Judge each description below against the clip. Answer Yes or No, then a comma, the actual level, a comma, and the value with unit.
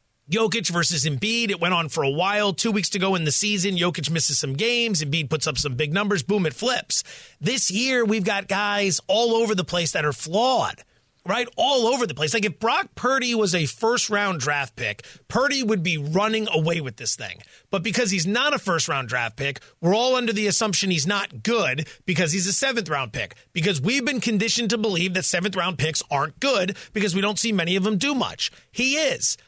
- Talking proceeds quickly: Yes, fast, 225 wpm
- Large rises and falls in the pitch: Yes, wide, 5.9 semitones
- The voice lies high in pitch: Yes, high, 195 Hz